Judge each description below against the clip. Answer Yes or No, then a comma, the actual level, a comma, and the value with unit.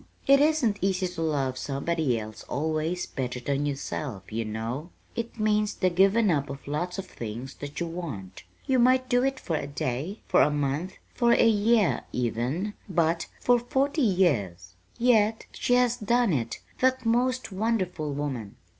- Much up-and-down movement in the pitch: Yes, wide, 8.6 semitones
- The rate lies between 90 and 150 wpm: No, average, 165 wpm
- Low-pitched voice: No, medium, 170 Hz